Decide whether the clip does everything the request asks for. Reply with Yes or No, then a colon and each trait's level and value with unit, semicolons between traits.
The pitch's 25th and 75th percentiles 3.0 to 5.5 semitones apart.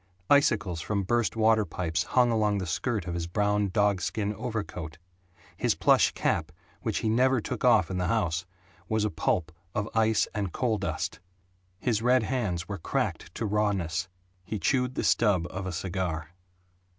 Yes: average, 3.8 semitones